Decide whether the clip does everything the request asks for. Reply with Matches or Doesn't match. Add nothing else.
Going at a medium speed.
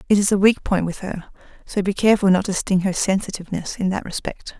Doesn't match